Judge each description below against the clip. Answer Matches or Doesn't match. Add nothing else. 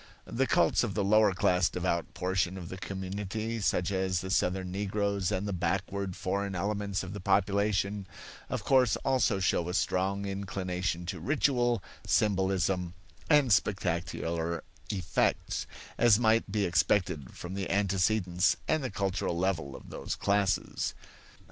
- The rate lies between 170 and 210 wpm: Doesn't match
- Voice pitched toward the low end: Matches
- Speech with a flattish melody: Matches